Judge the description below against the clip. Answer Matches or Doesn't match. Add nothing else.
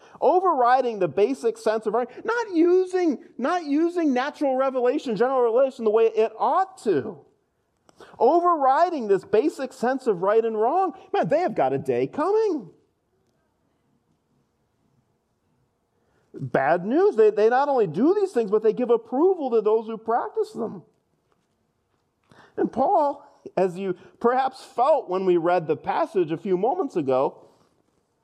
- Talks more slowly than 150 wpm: Matches